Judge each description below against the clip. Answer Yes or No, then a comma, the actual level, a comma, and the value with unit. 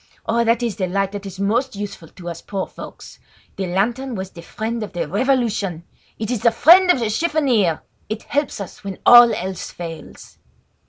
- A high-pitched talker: Yes, high, 210 Hz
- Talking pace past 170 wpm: Yes, average, 195 wpm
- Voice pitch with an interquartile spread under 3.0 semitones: No, average, 4.1 semitones